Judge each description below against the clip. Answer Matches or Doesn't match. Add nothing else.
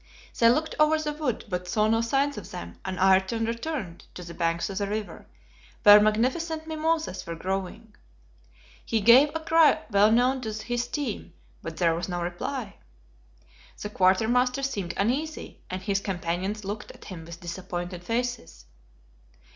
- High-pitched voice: Matches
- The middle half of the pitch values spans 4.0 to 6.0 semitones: Matches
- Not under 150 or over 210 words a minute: Matches